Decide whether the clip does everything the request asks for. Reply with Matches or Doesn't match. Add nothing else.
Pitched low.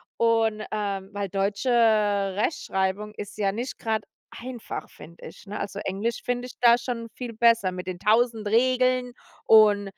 Doesn't match